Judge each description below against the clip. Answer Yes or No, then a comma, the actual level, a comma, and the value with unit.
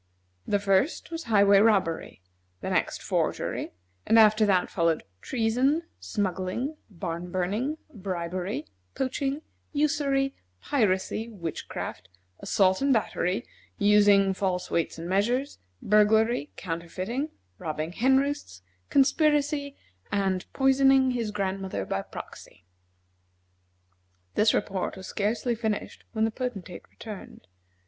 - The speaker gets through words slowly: Yes, slow, 110 wpm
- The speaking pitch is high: Yes, high, 210 Hz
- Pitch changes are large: Yes, wide, 5.8 semitones